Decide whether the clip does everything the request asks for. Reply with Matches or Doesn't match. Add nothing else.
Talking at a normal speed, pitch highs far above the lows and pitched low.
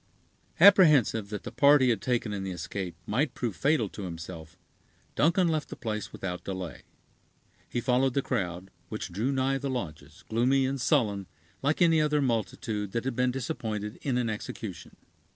Matches